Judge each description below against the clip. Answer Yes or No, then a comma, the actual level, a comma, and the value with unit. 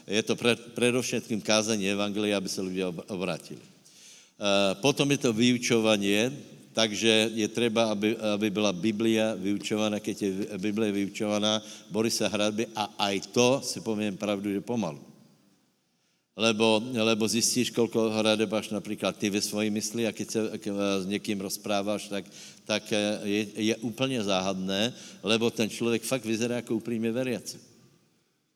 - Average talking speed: Yes, average, 150 wpm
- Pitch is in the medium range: No, low, 110 Hz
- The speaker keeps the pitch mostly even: Yes, narrow, 1.7 semitones